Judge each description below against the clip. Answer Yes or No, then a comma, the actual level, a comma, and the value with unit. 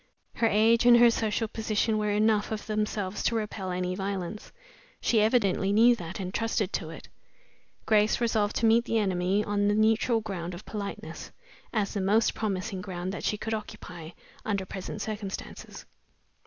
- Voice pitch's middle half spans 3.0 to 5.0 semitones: No, narrow, 2.5 semitones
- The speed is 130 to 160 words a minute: No, average, 170 wpm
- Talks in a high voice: Yes, high, 210 Hz